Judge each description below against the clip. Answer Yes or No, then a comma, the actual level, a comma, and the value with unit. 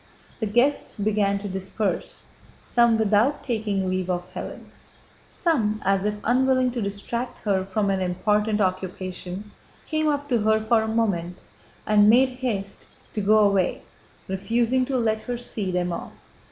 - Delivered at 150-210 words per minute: Yes, average, 155 wpm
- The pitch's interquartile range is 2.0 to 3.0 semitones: No, average, 3.5 semitones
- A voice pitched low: No, high, 210 Hz